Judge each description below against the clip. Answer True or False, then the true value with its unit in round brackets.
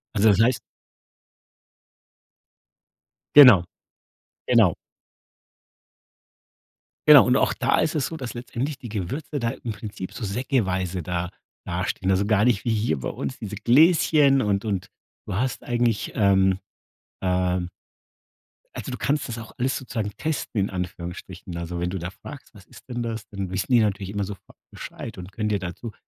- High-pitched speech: False (105 Hz)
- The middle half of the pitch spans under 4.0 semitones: False (4.8 semitones)